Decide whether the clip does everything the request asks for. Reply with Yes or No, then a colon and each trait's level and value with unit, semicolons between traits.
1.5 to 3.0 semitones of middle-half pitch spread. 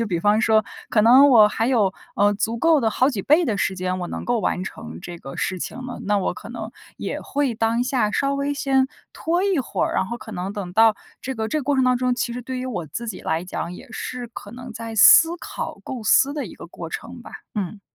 No: average, 4.2 semitones